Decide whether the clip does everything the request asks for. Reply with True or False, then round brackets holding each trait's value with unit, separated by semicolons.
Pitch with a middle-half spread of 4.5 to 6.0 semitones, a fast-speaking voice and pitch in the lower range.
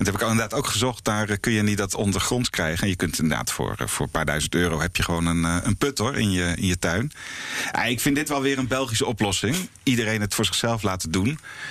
True (5.2 semitones; 245 wpm; 105 Hz)